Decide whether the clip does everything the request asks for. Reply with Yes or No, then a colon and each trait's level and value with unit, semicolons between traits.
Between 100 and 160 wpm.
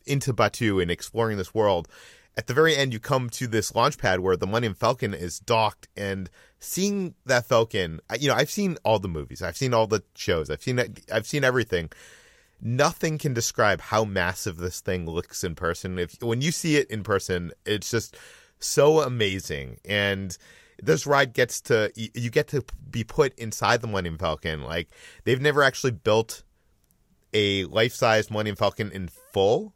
No: average, 180 wpm